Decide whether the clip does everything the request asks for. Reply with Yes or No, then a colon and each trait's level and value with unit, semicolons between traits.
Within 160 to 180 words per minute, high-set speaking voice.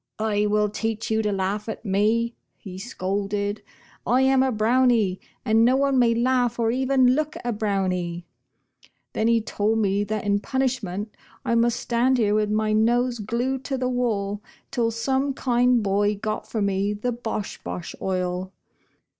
Yes: average, 170 wpm; high, 220 Hz